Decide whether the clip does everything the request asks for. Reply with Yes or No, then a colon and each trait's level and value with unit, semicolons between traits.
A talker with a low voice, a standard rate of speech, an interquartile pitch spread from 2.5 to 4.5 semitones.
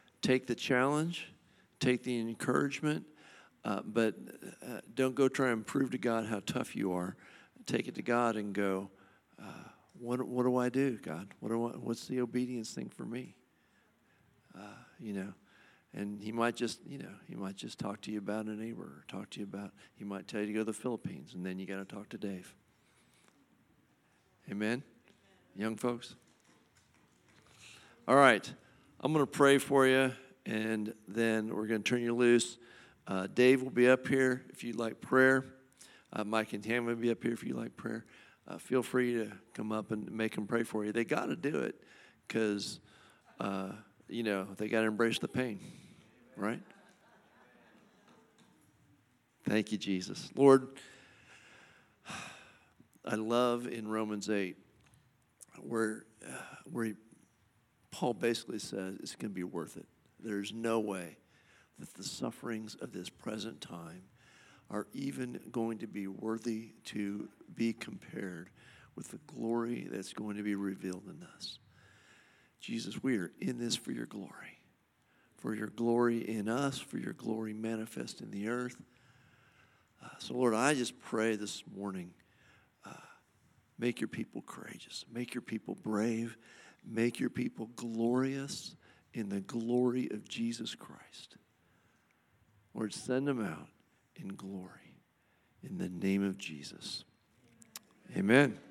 Yes: low, 115 Hz; average, 155 wpm; average, 2.8 semitones